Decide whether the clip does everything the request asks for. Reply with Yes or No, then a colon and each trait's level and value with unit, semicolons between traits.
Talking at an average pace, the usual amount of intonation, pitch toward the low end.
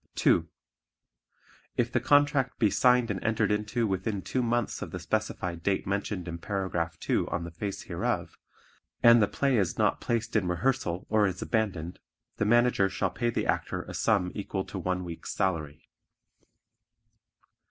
Yes: average, 165 wpm; average, 4.4 semitones; low, 100 Hz